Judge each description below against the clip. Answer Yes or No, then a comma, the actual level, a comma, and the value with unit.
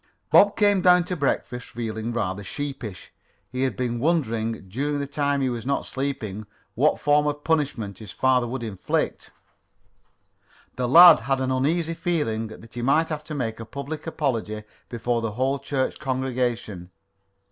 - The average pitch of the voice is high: No, low, 130 Hz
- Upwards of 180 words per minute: No, average, 160 wpm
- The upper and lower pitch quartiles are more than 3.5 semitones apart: Yes, average, 4.4 semitones